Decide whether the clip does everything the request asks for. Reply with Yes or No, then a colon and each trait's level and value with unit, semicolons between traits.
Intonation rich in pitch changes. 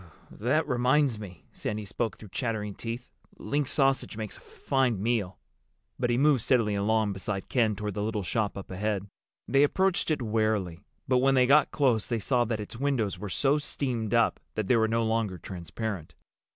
No: average, 3.6 semitones